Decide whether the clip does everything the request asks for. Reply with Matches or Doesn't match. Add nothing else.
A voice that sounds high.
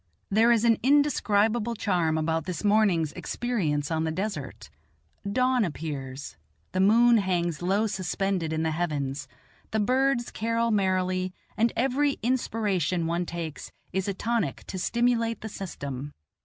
Matches